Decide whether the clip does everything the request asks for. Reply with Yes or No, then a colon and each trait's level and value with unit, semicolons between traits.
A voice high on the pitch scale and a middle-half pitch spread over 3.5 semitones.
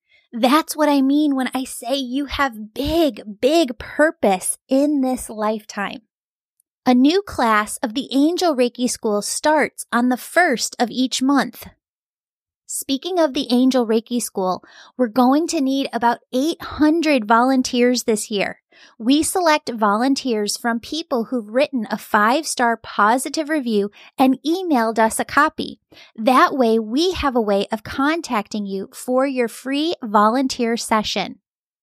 Yes: very high, 255 Hz; average, 4.1 semitones